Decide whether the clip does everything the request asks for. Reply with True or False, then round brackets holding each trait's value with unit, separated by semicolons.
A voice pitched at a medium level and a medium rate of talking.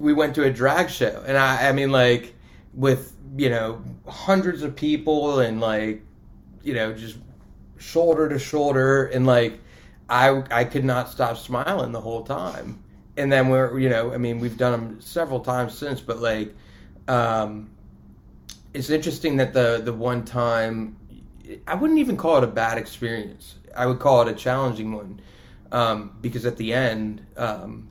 False (125 Hz; 170 wpm)